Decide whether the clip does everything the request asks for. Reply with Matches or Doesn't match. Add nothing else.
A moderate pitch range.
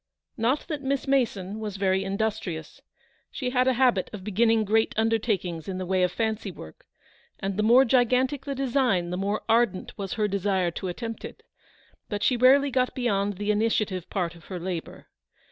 Matches